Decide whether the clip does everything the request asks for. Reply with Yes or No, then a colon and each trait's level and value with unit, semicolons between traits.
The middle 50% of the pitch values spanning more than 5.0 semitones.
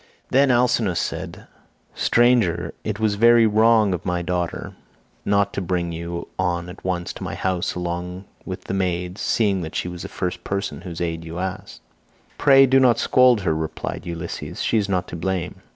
No: average, 3.9 semitones